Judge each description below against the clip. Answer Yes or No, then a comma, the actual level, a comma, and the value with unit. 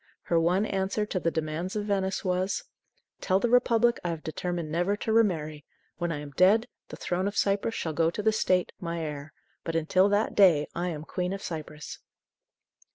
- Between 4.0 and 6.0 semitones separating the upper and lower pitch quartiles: No, average, 3.6 semitones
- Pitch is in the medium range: Yes, medium, 180 Hz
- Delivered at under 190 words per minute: No, average, 195 wpm